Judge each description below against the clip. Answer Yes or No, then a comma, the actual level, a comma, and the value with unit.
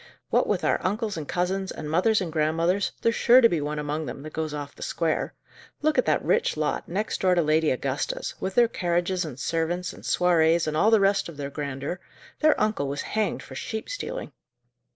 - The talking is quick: Yes, fast, 215 wpm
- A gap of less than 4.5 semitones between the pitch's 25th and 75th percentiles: No, average, 4.8 semitones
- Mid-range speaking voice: Yes, medium, 170 Hz